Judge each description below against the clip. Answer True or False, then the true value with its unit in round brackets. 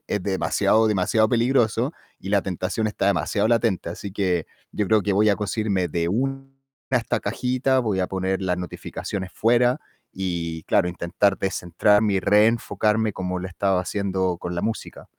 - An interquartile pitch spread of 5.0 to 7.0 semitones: False (3.2 semitones)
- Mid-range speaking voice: False (100 Hz)